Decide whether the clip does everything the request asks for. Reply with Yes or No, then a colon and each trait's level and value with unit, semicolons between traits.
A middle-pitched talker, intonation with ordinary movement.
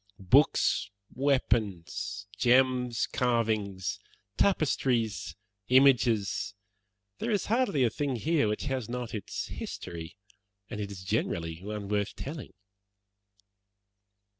No: low, 115 Hz; average, 4.5 semitones